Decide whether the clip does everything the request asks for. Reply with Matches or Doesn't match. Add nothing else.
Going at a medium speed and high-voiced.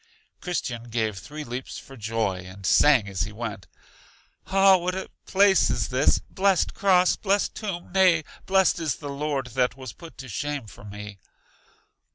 Doesn't match